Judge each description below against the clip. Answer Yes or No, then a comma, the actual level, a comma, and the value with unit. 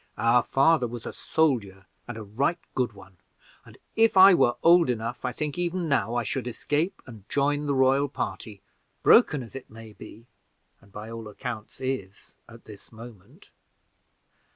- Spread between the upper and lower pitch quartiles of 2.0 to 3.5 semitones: No, average, 4.6 semitones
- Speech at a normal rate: Yes, average, 170 wpm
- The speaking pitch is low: Yes, low, 120 Hz